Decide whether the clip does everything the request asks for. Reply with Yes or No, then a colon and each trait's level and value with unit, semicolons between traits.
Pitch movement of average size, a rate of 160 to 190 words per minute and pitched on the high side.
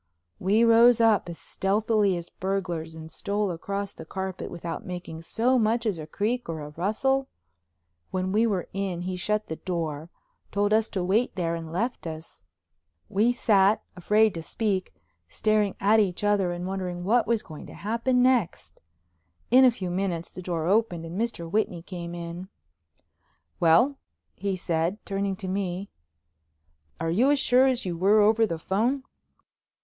Yes: average, 4.0 semitones; average, 165 wpm; high, 195 Hz